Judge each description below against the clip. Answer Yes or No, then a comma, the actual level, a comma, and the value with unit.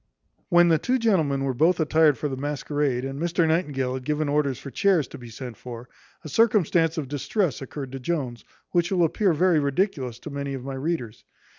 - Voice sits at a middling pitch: Yes, medium, 150 Hz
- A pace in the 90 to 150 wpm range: No, average, 200 wpm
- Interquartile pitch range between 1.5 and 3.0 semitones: No, average, 4.3 semitones